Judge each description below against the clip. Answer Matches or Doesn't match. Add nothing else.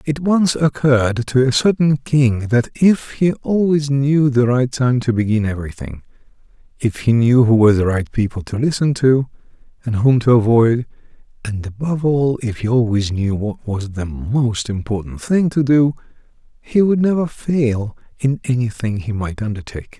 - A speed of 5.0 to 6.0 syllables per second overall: Doesn't match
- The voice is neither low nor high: Doesn't match